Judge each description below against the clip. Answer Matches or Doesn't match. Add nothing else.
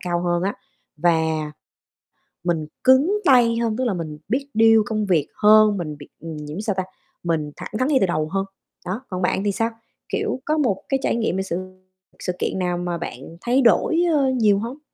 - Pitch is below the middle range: Doesn't match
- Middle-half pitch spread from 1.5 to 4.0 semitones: Doesn't match